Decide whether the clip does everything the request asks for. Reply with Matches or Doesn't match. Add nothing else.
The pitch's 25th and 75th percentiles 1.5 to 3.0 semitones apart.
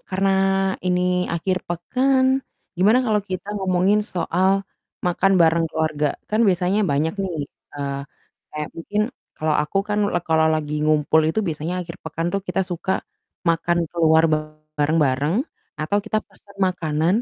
Doesn't match